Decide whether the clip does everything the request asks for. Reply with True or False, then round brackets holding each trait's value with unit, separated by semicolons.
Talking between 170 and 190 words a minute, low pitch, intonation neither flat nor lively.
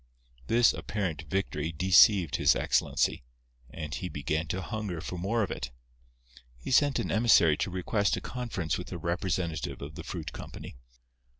False (160 wpm; 90 Hz; 4.3 semitones)